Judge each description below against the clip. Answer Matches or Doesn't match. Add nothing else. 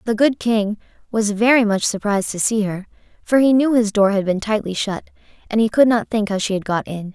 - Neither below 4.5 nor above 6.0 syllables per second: Matches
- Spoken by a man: Doesn't match